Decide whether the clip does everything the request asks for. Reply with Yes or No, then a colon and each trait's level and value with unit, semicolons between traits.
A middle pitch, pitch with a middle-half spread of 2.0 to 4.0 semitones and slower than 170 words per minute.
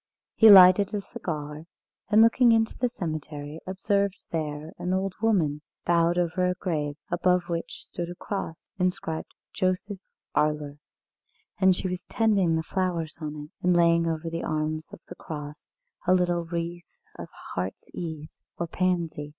Yes: medium, 170 Hz; average, 3.0 semitones; average, 155 wpm